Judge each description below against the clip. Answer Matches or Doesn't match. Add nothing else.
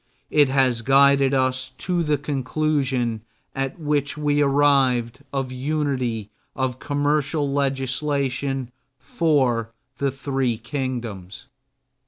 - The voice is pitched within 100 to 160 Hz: Matches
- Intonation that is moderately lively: Doesn't match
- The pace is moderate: Doesn't match